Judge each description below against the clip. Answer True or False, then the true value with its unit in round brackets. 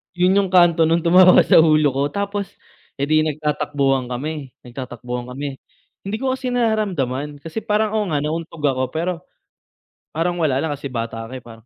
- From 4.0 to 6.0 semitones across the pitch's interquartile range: True (5.1 semitones)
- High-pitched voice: False (155 Hz)